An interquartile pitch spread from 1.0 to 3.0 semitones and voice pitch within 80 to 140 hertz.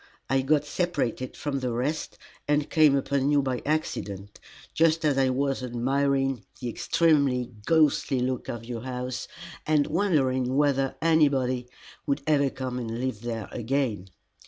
Yes: average, 2.7 semitones; low, 135 Hz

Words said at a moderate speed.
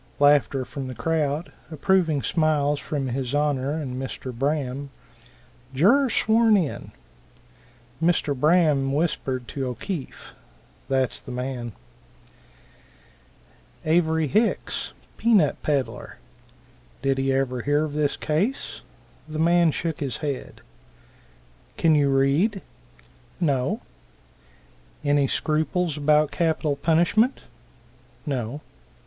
No: slow, 105 wpm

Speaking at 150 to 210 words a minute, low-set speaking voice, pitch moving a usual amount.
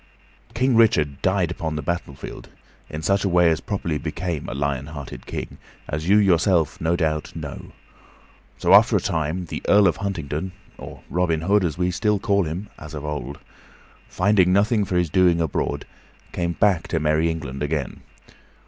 Yes: average, 175 wpm; very low, 85 Hz; average, 3.6 semitones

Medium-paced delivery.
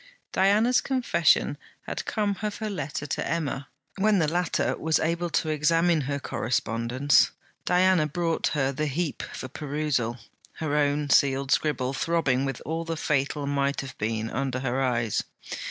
Yes: average, 155 wpm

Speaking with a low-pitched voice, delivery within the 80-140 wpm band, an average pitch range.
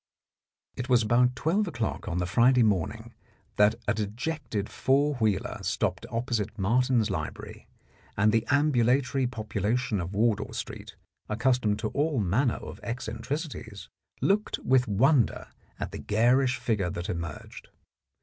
Yes: low, 115 Hz; slow, 135 wpm; average, 3.9 semitones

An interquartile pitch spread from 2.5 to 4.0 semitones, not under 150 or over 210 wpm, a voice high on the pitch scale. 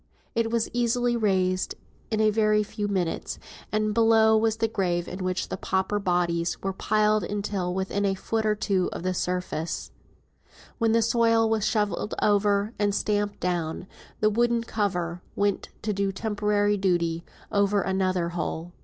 Yes: average, 2.9 semitones; average, 160 wpm; high, 205 Hz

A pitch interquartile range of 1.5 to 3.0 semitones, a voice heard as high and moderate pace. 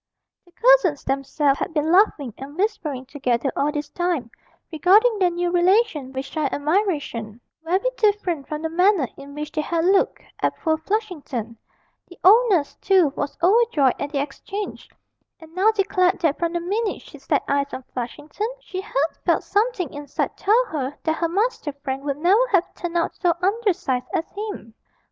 No: wide, 5.6 semitones; very high, 335 Hz; average, 175 wpm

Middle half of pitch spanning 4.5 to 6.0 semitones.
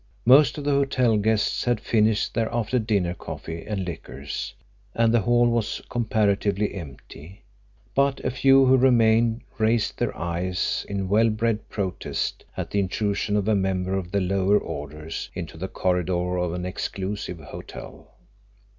No: average, 4.0 semitones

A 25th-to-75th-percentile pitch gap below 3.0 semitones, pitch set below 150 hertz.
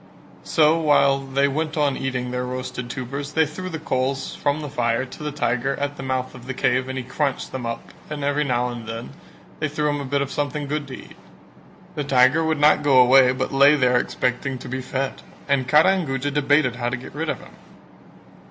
Yes: narrow, 2.6 semitones; low, 135 Hz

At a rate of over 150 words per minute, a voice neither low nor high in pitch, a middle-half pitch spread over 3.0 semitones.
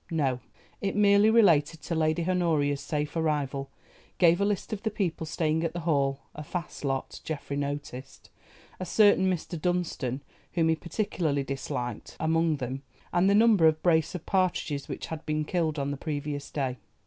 Yes: average, 165 wpm; medium, 160 Hz; average, 3.7 semitones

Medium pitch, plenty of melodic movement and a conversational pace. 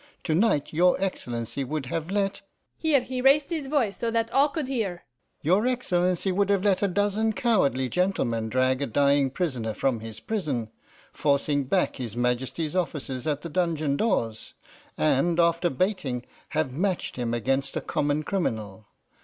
Yes: medium, 165 Hz; wide, 7.6 semitones; average, 160 wpm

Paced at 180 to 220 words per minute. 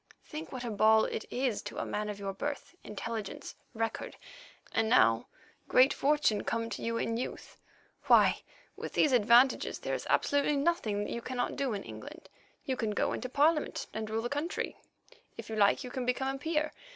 Yes: average, 190 wpm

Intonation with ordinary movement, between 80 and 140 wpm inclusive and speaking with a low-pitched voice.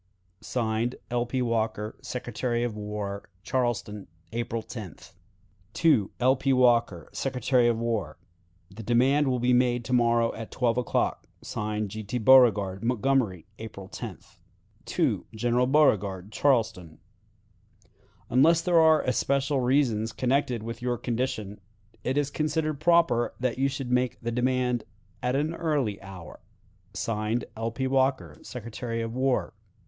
Yes: average, 3.1 semitones; slow, 135 wpm; low, 120 Hz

